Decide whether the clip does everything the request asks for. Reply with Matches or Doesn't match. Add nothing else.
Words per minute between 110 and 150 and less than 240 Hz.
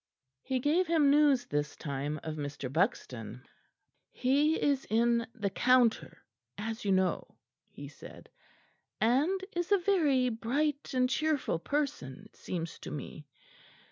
Doesn't match